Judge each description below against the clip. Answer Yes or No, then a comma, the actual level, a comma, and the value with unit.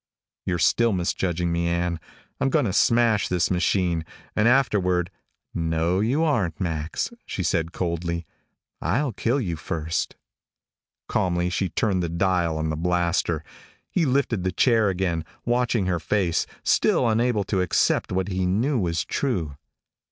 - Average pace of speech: Yes, average, 150 wpm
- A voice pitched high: No, very low, 90 Hz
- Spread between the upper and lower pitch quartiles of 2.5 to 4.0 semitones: No, average, 4.5 semitones